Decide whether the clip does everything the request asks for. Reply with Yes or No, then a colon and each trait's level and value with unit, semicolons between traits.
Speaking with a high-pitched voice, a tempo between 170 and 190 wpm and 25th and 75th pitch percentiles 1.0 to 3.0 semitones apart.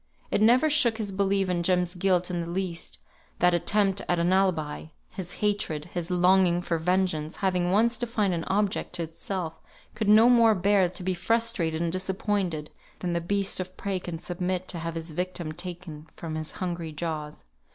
No: medium, 180 Hz; average, 185 wpm; narrow, 2.6 semitones